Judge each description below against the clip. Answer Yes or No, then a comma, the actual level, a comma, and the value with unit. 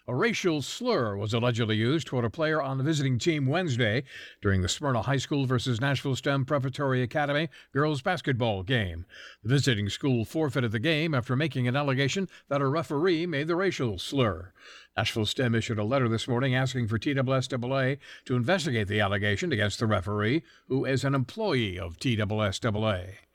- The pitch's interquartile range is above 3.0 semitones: Yes, average, 4.1 semitones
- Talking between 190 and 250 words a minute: No, average, 170 wpm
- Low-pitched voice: Yes, low, 130 Hz